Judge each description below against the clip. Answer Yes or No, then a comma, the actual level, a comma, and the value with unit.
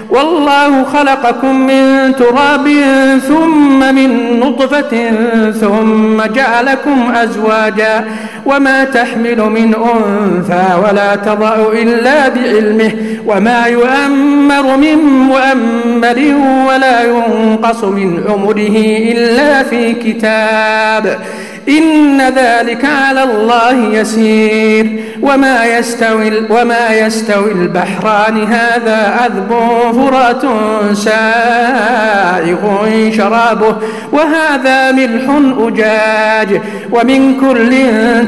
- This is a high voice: Yes, high, 235 Hz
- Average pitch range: Yes, average, 3.4 semitones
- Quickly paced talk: No, average, 75 wpm